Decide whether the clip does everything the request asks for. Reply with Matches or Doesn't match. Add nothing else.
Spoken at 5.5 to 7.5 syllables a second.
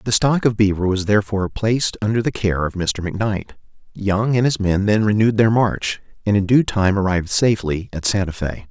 Matches